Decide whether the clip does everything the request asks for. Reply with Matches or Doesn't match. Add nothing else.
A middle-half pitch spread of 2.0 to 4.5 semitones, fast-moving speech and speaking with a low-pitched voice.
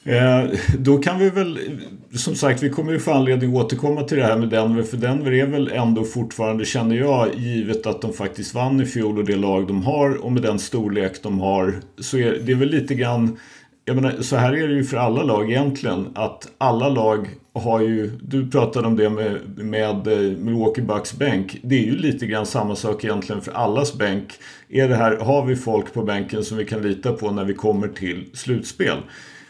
Matches